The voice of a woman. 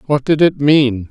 No: male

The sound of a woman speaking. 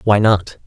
No: male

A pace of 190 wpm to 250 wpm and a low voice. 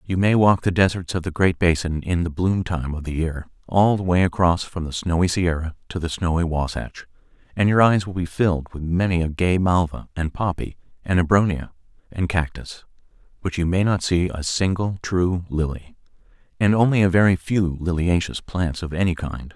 Yes: average, 195 wpm; very low, 90 Hz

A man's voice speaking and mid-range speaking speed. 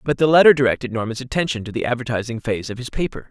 No: male; fast, 235 wpm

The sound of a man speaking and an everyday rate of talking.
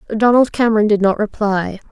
No: female; average, 155 wpm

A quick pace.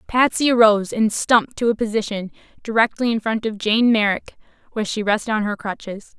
No: average, 185 wpm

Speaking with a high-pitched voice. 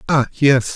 No: low, 135 Hz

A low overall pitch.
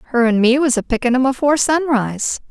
No: very high, 255 Hz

